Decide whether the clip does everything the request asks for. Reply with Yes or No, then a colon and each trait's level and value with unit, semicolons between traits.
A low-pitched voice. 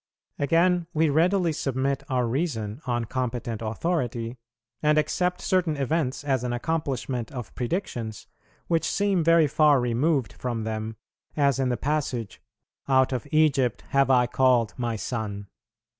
Yes: low, 130 Hz